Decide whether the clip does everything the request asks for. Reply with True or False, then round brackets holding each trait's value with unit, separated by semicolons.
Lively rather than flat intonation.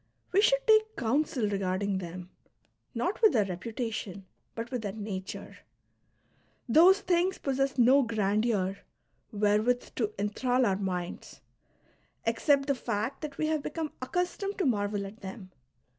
True (6.2 semitones)